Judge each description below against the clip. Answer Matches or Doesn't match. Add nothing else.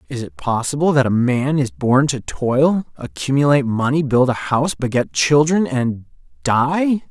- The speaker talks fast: Doesn't match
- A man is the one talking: Matches